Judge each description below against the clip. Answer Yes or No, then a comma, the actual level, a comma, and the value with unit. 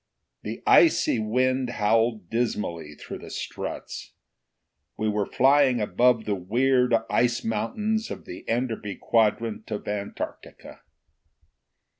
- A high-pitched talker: No, low, 115 Hz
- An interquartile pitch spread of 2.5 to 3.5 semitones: Yes, average, 3.1 semitones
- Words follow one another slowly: Yes, slow, 110 wpm